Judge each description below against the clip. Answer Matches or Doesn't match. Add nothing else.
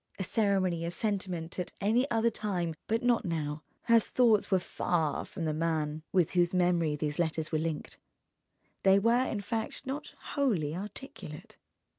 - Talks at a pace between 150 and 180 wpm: Matches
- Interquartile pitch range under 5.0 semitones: Doesn't match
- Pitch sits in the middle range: Matches